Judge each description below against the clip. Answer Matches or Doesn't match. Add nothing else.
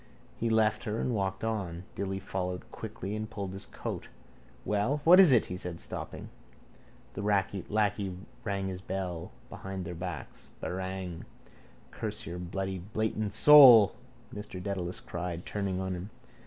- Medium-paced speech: Matches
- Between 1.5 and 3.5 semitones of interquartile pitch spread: Matches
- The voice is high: Doesn't match